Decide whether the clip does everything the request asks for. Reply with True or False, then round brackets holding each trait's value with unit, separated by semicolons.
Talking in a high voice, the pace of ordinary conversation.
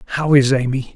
False (135 Hz; 190 wpm)